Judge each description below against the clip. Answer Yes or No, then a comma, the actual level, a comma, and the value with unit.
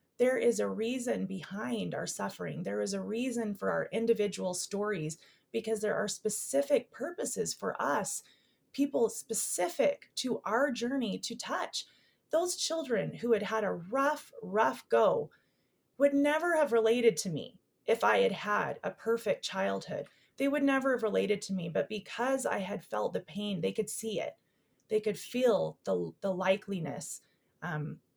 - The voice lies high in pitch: Yes, high, 220 Hz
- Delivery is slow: No, average, 160 wpm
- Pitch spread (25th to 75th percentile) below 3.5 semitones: No, average, 4.5 semitones